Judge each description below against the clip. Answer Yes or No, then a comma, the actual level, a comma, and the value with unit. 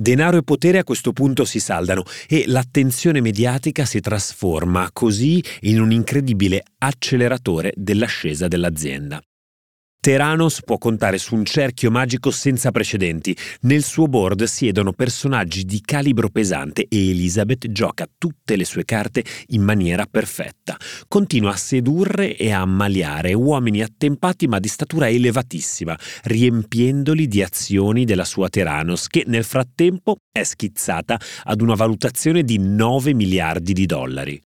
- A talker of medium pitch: No, low, 115 Hz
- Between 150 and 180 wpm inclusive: No, average, 135 wpm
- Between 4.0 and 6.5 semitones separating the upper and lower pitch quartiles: Yes, wide, 5.5 semitones